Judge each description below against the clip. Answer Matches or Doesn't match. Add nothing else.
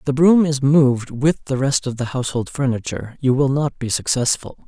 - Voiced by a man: Matches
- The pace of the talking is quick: Matches